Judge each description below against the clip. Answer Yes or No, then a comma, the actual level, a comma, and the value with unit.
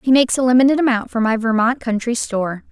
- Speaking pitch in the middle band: No, high, 240 Hz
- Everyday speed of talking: No, fast, 220 wpm